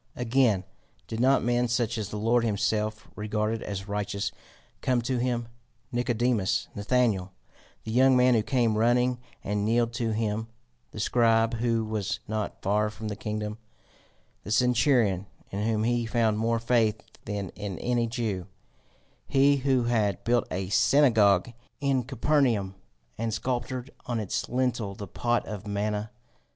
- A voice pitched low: Yes, low, 115 Hz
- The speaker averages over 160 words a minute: No, average, 145 wpm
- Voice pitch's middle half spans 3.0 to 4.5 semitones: No, narrow, 2.6 semitones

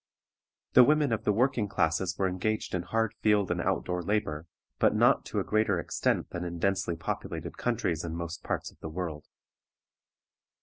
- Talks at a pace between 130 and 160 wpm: No, average, 180 wpm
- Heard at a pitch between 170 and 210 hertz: No, very low, 95 Hz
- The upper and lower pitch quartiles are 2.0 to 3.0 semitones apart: No, average, 4.2 semitones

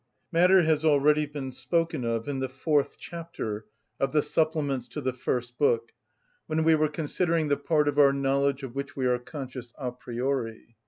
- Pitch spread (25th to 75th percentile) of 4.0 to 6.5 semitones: No, average, 3.3 semitones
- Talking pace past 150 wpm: Yes, average, 180 wpm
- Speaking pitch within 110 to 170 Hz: Yes, medium, 140 Hz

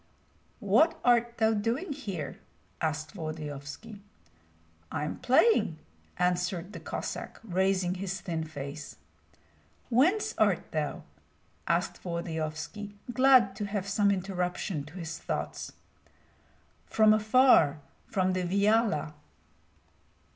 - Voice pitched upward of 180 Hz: Yes, high, 190 Hz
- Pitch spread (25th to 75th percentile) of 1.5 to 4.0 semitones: No, average, 5.3 semitones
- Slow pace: Yes, slow, 105 wpm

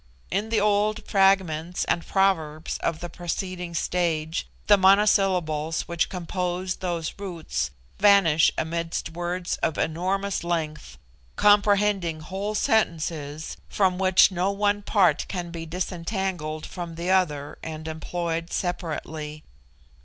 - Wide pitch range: No, average, 3.3 semitones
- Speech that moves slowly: Yes, slow, 115 wpm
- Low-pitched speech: No, medium, 175 Hz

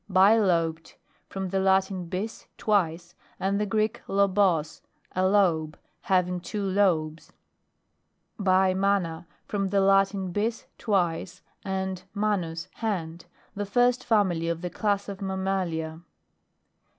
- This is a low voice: No, high, 190 Hz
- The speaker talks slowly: Yes, slow, 115 wpm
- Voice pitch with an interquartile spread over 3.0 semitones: No, average, 2.7 semitones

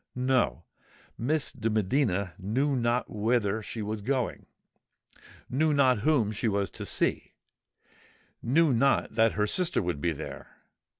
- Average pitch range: Yes, average, 4.6 semitones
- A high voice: No, low, 115 Hz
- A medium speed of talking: No, slow, 120 wpm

